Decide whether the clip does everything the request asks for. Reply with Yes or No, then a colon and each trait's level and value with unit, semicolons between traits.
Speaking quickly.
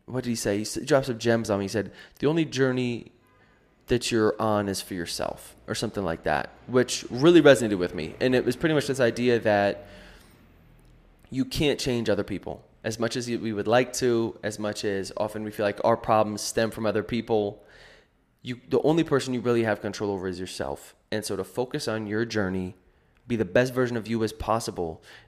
Yes: fast, 210 wpm